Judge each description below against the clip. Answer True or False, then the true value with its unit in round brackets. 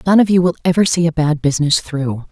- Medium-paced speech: False (260 wpm)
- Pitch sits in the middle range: True (160 Hz)